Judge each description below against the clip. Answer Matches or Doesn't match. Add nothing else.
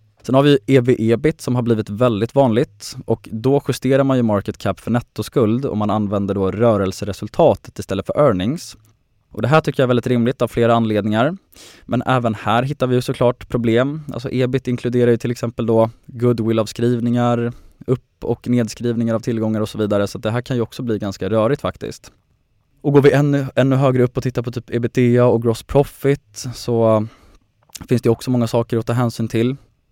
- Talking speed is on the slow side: Doesn't match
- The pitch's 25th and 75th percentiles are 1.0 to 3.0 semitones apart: Matches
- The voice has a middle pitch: Doesn't match